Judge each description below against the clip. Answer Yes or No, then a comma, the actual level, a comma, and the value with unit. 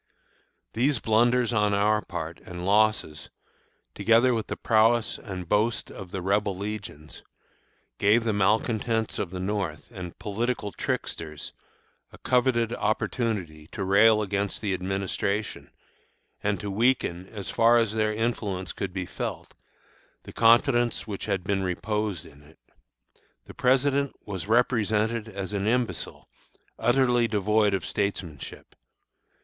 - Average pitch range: Yes, average, 3.2 semitones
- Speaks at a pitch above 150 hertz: No, low, 105 Hz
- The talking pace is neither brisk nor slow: No, slow, 130 wpm